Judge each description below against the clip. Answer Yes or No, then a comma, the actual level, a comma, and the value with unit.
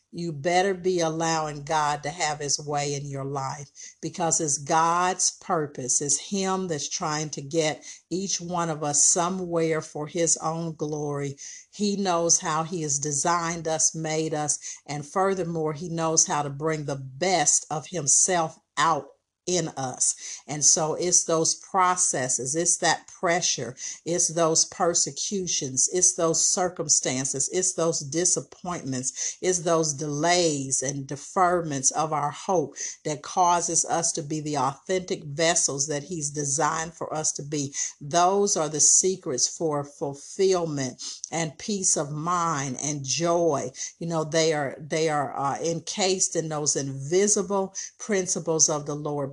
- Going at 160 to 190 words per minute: No, average, 145 wpm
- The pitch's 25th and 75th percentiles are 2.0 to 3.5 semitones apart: Yes, average, 2.9 semitones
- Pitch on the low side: No, medium, 160 Hz